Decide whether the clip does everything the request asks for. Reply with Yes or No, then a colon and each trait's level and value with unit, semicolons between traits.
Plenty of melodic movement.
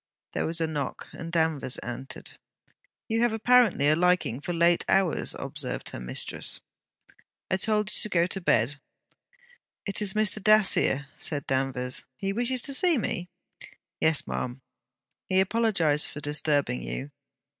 Yes: wide, 7.1 semitones